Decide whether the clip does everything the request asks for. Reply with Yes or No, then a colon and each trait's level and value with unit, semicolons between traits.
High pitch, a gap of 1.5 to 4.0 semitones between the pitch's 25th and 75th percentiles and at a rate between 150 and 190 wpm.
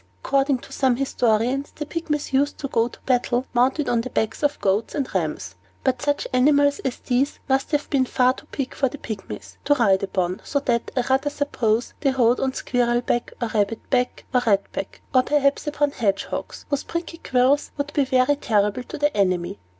No: very high, 255 Hz; average, 3.7 semitones; fast, 205 wpm